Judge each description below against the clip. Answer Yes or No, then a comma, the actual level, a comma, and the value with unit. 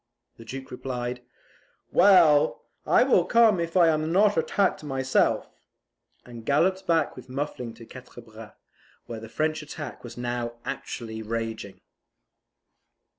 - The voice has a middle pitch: No, low, 130 Hz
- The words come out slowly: Yes, slow, 130 wpm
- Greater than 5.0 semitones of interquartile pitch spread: Yes, wide, 5.6 semitones